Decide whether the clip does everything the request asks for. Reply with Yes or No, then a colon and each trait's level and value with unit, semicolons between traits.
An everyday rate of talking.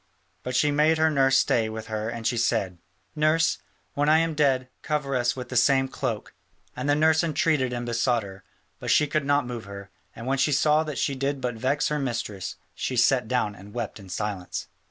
No: fast, 215 wpm